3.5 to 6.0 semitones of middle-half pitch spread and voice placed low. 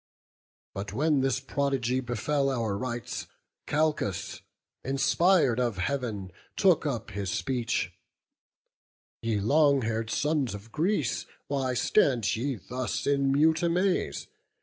Yes: average, 4.3 semitones; low, 130 Hz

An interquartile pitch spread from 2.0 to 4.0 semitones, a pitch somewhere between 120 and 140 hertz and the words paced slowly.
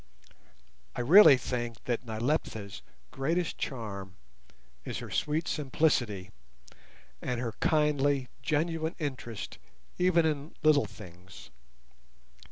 No: wide, 5.4 semitones; low, 135 Hz; slow, 95 wpm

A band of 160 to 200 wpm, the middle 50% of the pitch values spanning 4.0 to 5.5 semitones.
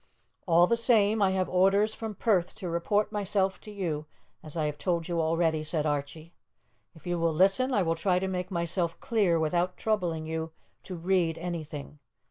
No: average, 185 wpm; average, 3.2 semitones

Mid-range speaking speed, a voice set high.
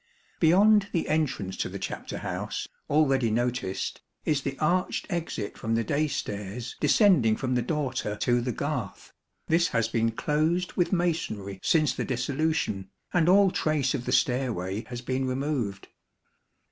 No: average, 150 wpm; low, 130 Hz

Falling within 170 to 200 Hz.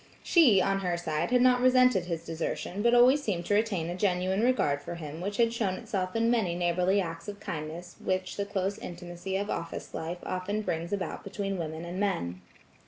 Yes: medium, 185 Hz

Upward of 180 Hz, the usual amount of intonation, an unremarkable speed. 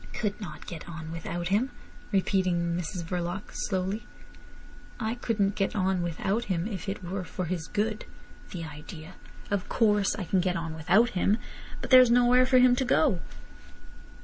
Yes: high, 190 Hz; average, 3.8 semitones; average, 165 wpm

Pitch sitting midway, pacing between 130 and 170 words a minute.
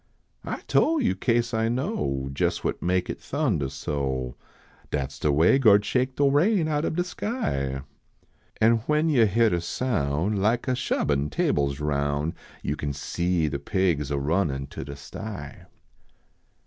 No: very low, 90 Hz; average, 160 wpm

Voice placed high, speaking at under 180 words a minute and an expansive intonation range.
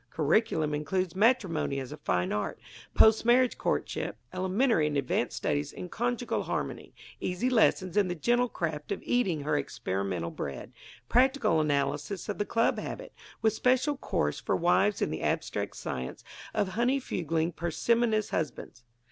No: medium, 180 Hz; average, 150 wpm; wide, 7.7 semitones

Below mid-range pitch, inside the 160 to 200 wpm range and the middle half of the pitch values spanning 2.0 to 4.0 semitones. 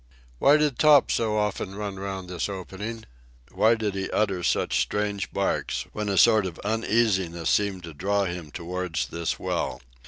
Yes: low, 100 Hz; average, 165 wpm; average, 2.9 semitones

